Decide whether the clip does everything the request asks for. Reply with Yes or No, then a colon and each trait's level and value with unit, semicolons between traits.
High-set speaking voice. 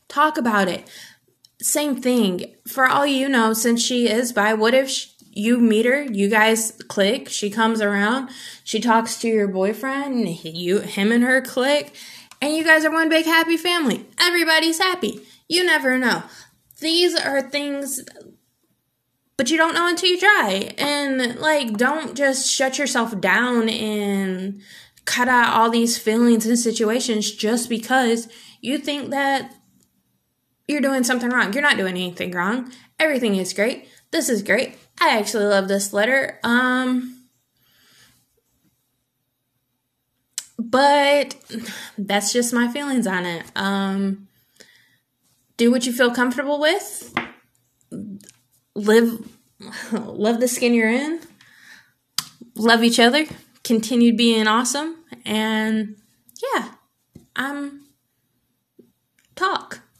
Yes: high, 235 Hz